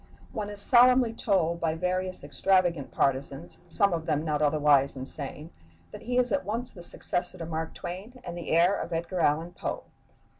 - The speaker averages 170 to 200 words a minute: Yes, average, 180 wpm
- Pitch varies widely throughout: No, average, 4.5 semitones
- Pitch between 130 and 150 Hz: No, medium, 170 Hz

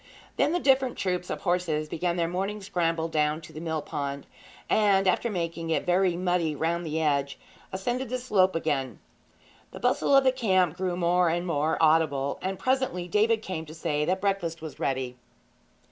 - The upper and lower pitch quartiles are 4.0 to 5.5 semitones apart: No, average, 3.3 semitones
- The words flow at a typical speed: Yes, average, 180 wpm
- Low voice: No, medium, 175 Hz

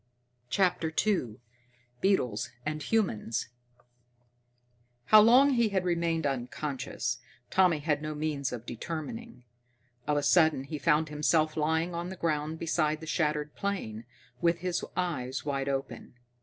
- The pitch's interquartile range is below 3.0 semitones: No, average, 3.6 semitones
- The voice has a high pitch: No, medium, 155 Hz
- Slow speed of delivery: Yes, slow, 130 wpm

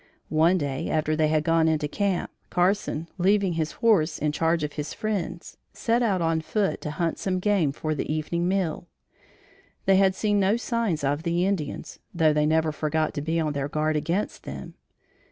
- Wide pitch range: No, average, 3.7 semitones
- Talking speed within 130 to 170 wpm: No, average, 185 wpm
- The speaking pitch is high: No, medium, 165 Hz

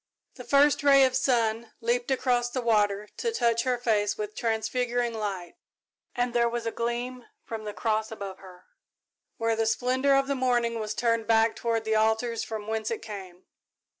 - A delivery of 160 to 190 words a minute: Yes, average, 180 wpm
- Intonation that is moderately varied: No, narrow, 2.1 semitones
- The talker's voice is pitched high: Yes, high, 230 Hz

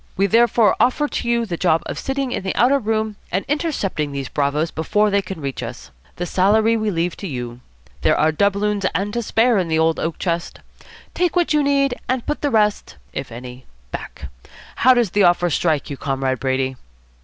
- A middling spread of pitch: No, wide, 6.8 semitones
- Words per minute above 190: Yes, average, 200 wpm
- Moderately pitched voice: No, high, 195 Hz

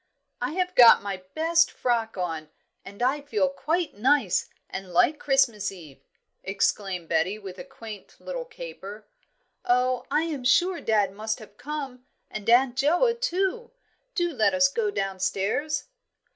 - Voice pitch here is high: Yes, very high, 250 Hz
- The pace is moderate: Yes, average, 145 wpm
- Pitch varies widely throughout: Yes, wide, 7.7 semitones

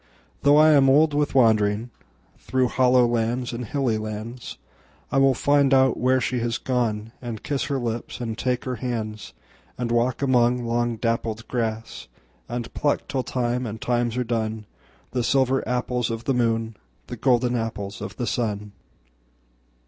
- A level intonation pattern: Yes, narrow, 2.3 semitones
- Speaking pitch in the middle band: No, low, 120 Hz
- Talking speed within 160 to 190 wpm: No, average, 140 wpm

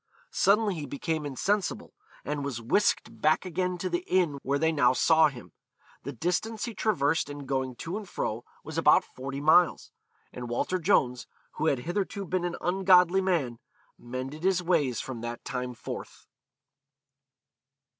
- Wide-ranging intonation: Yes, wide, 5.7 semitones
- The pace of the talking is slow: No, average, 155 wpm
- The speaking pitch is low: No, medium, 155 Hz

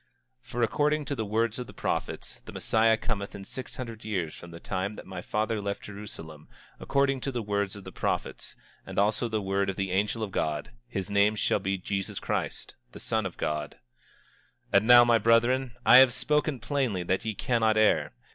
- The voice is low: Yes, low, 110 Hz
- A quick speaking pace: Yes, fast, 210 wpm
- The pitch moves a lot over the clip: No, average, 3.5 semitones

